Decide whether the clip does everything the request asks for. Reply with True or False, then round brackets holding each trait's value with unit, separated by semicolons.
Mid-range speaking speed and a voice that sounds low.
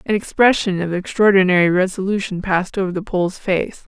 False (150 wpm; 190 Hz)